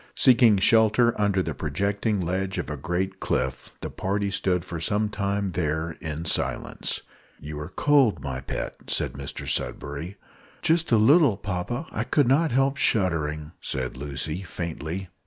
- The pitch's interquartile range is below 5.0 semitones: No, wide, 5.6 semitones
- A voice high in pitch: No, very low, 95 Hz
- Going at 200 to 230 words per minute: No, average, 155 wpm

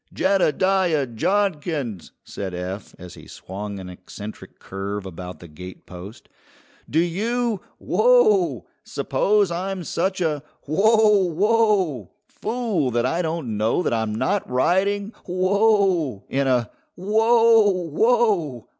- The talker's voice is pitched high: No, medium, 170 Hz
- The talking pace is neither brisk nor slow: No, slow, 115 wpm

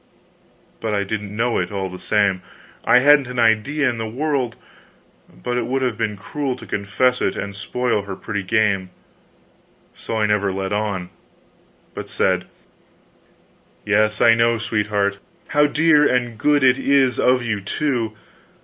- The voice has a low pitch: Yes, low, 115 Hz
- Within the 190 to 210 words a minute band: No, average, 160 wpm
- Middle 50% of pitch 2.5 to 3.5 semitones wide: No, average, 3.9 semitones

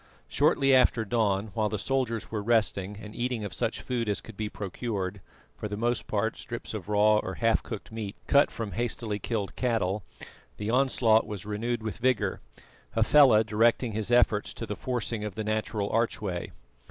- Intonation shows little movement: Yes, narrow, 2.3 semitones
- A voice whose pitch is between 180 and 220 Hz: No, low, 110 Hz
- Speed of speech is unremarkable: Yes, average, 175 wpm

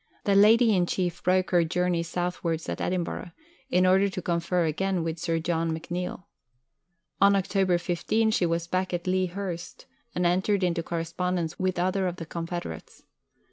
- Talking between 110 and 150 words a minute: No, average, 165 wpm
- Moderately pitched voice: Yes, medium, 180 Hz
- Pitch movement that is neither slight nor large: No, narrow, 1.8 semitones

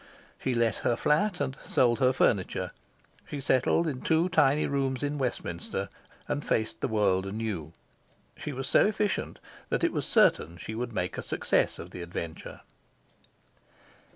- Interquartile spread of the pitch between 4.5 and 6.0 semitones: Yes, wide, 5.5 semitones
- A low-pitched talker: Yes, low, 125 Hz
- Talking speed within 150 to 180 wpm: Yes, average, 155 wpm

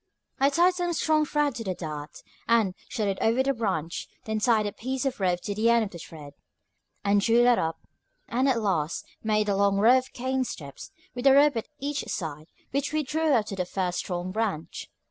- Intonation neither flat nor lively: No, wide, 5.9 semitones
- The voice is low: No, high, 225 Hz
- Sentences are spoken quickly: Yes, fast, 220 wpm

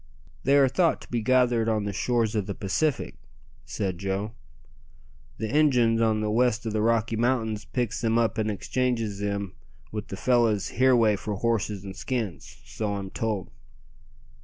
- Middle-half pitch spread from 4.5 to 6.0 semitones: No, average, 2.9 semitones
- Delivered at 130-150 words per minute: No, average, 165 wpm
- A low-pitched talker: Yes, low, 110 Hz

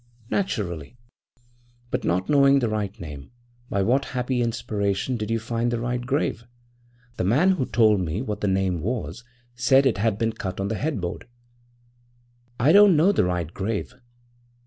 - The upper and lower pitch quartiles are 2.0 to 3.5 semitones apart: No, average, 4.7 semitones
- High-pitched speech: No, low, 115 Hz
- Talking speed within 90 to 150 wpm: No, average, 165 wpm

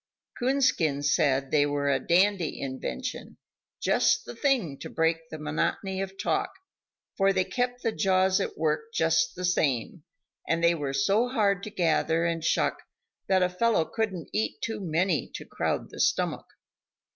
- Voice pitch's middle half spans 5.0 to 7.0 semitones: No, average, 4.5 semitones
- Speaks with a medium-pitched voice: Yes, medium, 170 Hz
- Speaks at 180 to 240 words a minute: No, average, 160 wpm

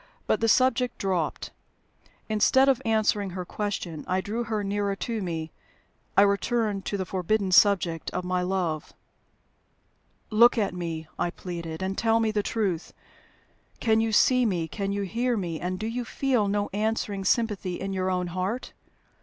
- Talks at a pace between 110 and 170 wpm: Yes, average, 165 wpm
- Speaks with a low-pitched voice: No, high, 200 Hz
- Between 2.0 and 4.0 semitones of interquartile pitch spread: Yes, average, 3.5 semitones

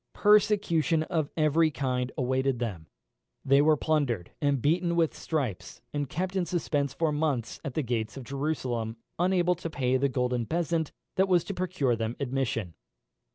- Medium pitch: Yes, medium, 145 Hz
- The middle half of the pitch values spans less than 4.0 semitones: No, average, 4.8 semitones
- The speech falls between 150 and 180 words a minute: Yes, average, 160 wpm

